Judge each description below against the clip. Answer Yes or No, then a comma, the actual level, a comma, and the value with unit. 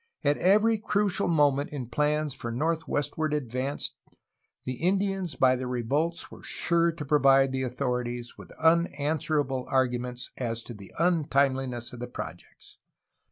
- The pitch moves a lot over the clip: No, average, 4.4 semitones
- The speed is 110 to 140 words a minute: Yes, slow, 135 wpm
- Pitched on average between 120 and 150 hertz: Yes, medium, 140 Hz